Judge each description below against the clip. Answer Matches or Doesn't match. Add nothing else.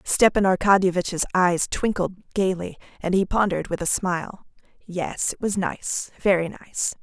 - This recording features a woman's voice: Matches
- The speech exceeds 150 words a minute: Doesn't match